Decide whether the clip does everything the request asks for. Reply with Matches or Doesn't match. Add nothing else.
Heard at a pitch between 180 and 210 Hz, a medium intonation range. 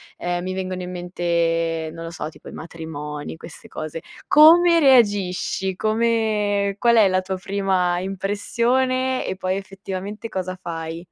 Matches